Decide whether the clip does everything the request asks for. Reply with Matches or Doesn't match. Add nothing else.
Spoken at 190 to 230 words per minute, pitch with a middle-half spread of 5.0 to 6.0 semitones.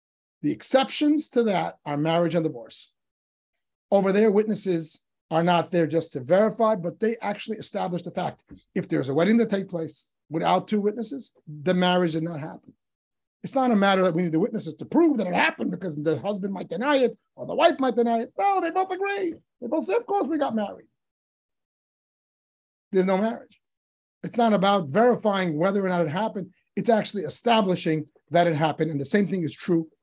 Matches